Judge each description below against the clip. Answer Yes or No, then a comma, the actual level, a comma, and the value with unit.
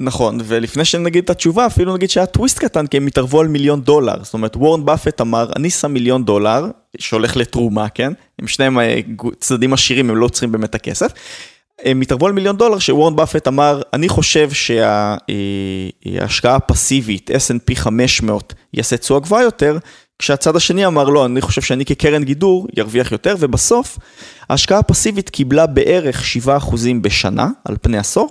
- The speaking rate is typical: No, fast, 160 wpm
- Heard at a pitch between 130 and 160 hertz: Yes, low, 135 Hz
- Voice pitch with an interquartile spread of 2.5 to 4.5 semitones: No, average, 5.2 semitones